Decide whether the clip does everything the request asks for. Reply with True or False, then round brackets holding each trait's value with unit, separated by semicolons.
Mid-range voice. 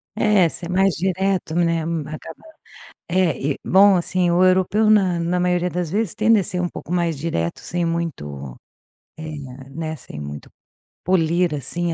True (175 Hz)